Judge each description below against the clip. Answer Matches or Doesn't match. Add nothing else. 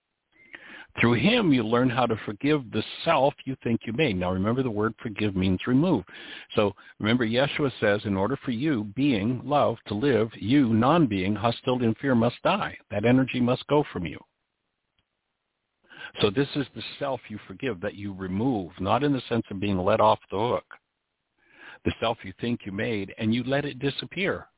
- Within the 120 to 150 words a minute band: Doesn't match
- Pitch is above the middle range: Doesn't match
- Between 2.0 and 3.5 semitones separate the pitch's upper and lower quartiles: Doesn't match